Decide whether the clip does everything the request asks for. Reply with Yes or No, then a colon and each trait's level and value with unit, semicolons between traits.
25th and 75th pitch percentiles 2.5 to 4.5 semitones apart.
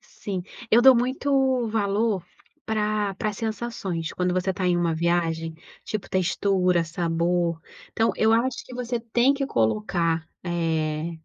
No: average, 5.0 semitones